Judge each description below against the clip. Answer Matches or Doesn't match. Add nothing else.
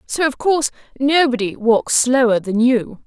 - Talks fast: Doesn't match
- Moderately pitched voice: Doesn't match